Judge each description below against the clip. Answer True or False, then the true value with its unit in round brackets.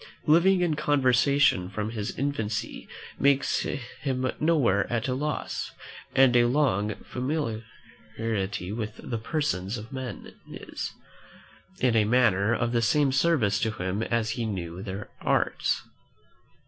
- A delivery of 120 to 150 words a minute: True (135 wpm)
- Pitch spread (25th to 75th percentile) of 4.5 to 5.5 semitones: True (4.8 semitones)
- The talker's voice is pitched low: True (120 Hz)